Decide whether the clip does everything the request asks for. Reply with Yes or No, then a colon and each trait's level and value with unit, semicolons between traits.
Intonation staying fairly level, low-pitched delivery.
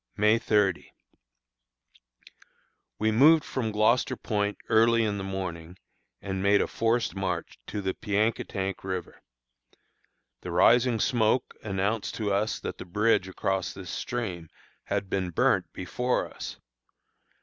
No: average, 3.0 semitones; low, 105 Hz